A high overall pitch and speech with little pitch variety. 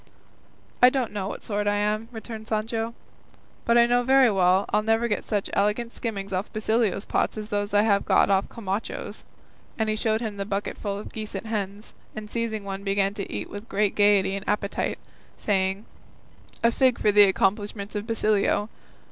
Yes: high, 210 Hz; narrow, 1.9 semitones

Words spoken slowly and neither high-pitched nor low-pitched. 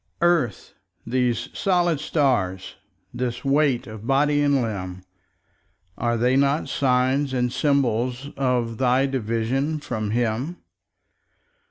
No: slow, 105 wpm; low, 125 Hz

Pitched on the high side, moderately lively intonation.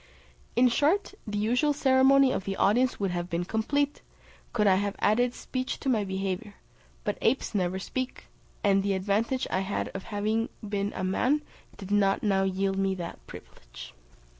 Yes: high, 205 Hz; average, 4.5 semitones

